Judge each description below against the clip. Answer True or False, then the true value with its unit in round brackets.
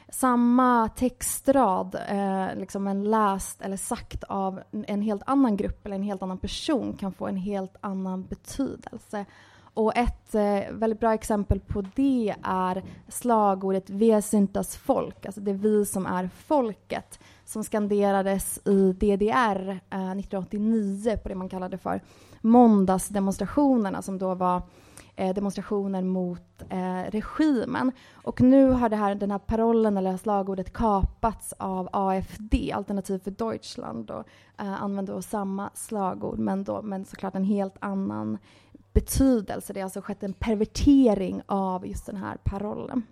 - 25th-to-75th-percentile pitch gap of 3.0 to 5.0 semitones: False (2.5 semitones)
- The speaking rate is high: False (140 wpm)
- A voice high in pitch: True (200 Hz)